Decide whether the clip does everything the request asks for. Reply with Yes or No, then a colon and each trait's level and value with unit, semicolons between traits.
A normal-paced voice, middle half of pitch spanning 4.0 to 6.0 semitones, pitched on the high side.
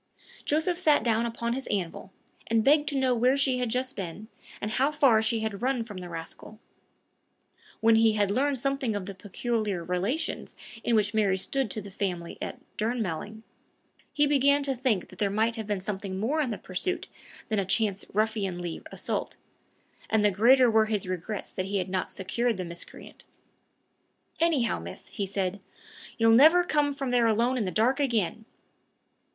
Yes: average, 180 wpm; average, 4.5 semitones; high, 220 Hz